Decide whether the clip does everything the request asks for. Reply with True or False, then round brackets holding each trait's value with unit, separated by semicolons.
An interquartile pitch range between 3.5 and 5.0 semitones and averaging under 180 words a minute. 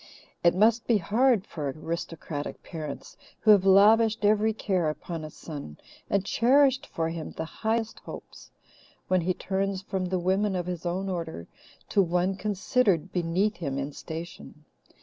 True (4.1 semitones; 155 wpm)